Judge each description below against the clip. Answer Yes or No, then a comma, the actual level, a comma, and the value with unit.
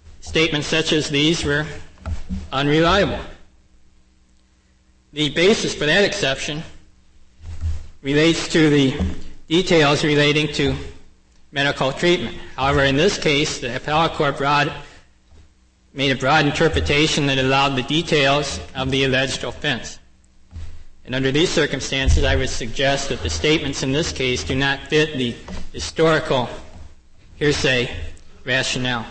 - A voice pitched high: No, low, 135 Hz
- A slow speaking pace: Yes, slow, 120 wpm